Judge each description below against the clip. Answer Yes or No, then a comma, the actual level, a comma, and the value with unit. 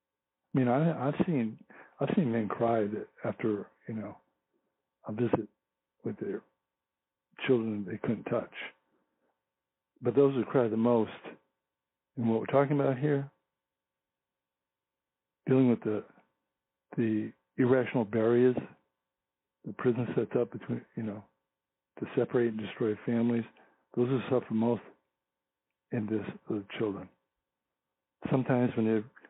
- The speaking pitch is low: Yes, low, 100 Hz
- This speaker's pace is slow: Yes, slow, 130 wpm